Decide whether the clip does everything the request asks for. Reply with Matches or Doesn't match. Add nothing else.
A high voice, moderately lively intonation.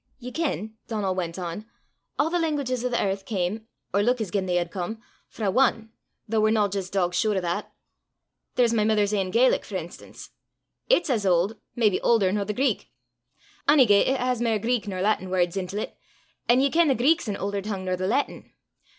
Matches